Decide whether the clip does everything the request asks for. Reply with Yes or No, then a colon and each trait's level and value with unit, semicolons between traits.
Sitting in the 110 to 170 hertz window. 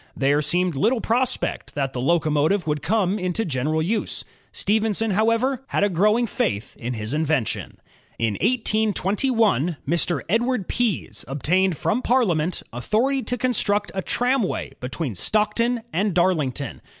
No: high, 190 Hz